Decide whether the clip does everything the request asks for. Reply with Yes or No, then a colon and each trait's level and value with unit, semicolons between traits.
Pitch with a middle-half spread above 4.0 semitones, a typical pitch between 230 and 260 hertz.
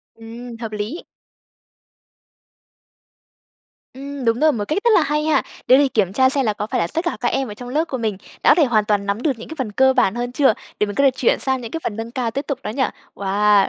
Yes: average, 4.6 semitones; high, 245 Hz